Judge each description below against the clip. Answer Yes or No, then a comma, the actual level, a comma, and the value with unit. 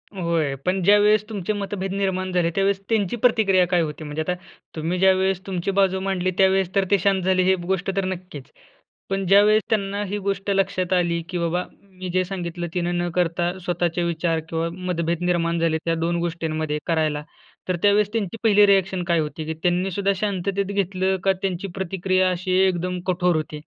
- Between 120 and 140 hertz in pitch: No, medium, 185 Hz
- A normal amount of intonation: No, narrow, 2.2 semitones